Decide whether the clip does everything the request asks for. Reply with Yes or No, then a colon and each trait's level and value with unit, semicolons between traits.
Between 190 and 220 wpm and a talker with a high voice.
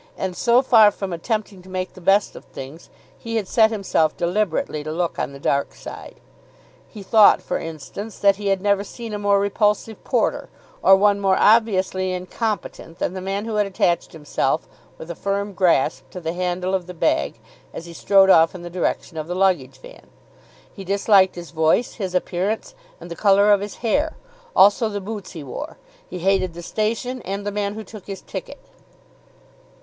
Yes: average, 195 wpm; high, 195 Hz